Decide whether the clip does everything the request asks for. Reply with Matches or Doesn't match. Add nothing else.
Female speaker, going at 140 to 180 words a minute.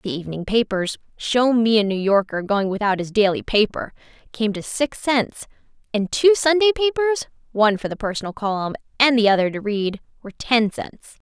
Matches